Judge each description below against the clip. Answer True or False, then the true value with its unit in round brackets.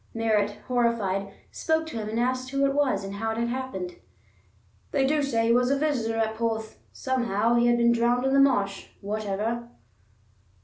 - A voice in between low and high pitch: False (235 Hz)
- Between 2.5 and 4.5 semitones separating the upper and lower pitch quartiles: True (3.2 semitones)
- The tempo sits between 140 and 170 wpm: False (185 wpm)